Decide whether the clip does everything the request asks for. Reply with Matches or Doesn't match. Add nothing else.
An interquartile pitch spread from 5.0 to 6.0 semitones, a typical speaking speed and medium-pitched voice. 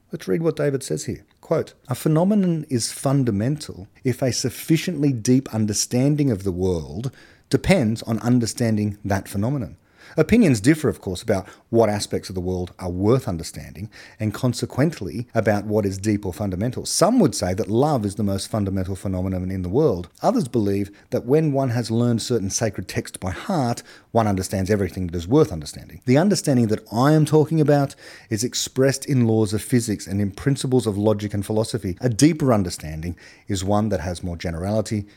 Doesn't match